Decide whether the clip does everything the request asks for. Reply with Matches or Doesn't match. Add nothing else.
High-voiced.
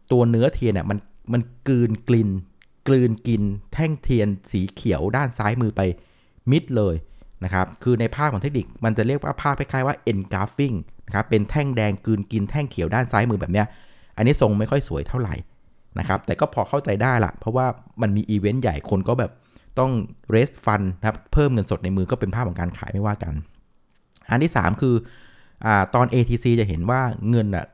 Doesn't match